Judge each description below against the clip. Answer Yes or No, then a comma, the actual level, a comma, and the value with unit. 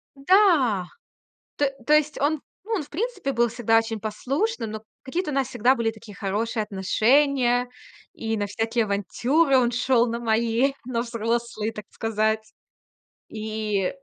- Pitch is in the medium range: No, high, 235 Hz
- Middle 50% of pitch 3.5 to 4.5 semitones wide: Yes, average, 4.0 semitones